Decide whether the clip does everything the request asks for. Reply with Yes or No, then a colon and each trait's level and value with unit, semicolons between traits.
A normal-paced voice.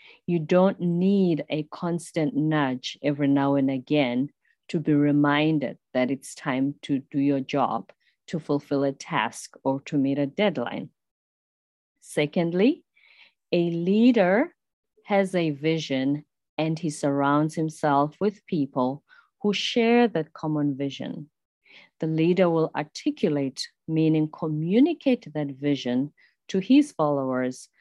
No: slow, 125 wpm